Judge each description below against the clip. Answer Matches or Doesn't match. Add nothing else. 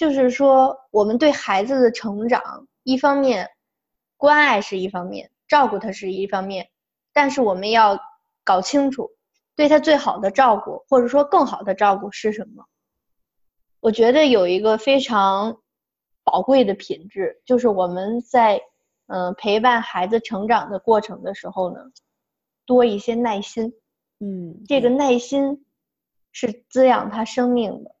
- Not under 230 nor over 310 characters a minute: Doesn't match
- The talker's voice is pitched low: Doesn't match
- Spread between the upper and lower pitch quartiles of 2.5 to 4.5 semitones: Doesn't match